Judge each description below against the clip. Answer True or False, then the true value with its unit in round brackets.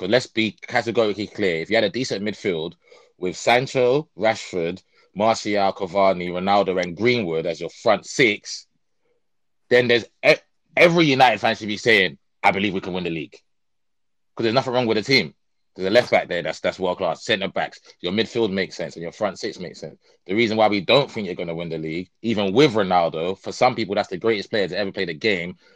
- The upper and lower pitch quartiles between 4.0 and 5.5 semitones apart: True (4.3 semitones)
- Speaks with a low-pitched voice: True (110 Hz)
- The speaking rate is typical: False (215 wpm)